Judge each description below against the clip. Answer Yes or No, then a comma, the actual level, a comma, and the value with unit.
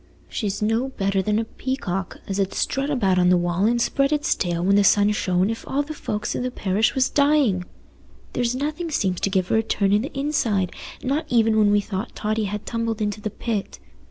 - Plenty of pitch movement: No, average, 4.5 semitones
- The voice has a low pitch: No, high, 215 Hz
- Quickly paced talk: Yes, fast, 220 wpm